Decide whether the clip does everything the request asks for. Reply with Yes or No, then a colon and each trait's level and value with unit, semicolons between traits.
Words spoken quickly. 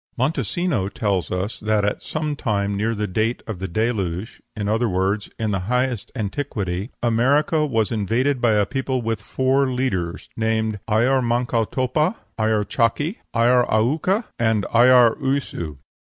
No: average, 150 wpm